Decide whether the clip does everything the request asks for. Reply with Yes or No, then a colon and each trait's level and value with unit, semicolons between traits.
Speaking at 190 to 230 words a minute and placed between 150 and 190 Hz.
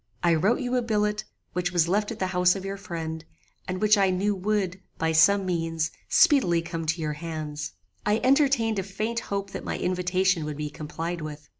Yes: average, 200 wpm; medium, 185 Hz